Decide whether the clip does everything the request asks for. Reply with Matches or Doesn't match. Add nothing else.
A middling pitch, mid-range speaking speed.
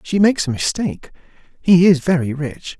Matches